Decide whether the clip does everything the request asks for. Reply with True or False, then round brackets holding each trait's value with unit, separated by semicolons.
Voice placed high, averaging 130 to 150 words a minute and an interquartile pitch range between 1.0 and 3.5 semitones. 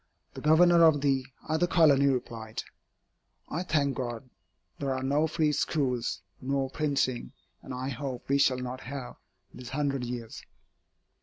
False (135 Hz; 145 wpm; 2.8 semitones)